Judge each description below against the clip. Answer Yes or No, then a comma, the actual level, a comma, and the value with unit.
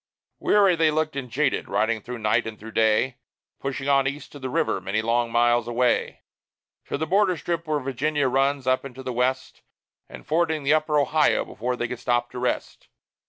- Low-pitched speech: Yes, low, 130 Hz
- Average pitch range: Yes, average, 4.0 semitones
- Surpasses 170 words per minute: Yes, average, 195 wpm